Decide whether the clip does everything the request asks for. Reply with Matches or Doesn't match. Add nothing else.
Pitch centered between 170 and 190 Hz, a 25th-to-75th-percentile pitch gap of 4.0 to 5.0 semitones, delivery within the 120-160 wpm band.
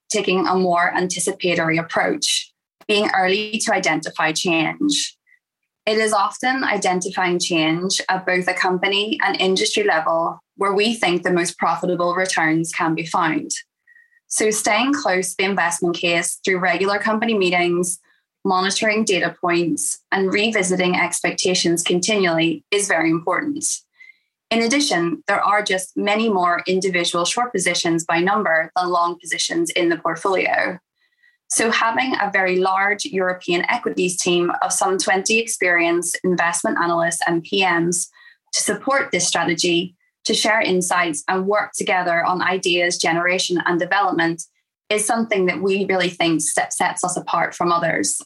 Doesn't match